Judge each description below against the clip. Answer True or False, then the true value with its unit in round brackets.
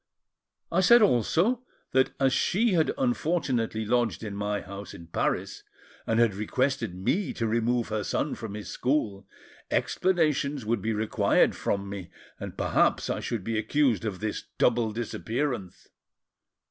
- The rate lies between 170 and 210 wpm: False (145 wpm)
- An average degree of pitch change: False (5.8 semitones)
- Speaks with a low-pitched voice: True (115 Hz)